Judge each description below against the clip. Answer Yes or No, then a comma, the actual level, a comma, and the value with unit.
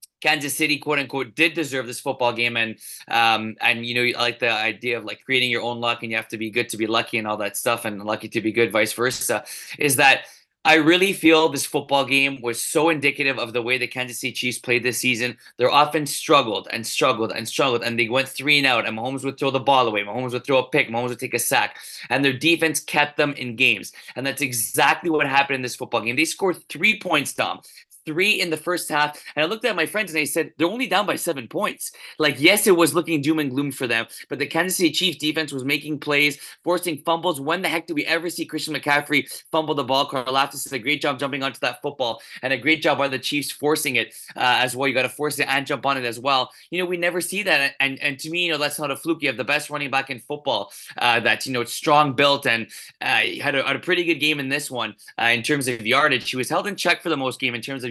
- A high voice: No, medium, 140 Hz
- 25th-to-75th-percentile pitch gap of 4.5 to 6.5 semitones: No, average, 3.9 semitones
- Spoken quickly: Yes, fast, 275 wpm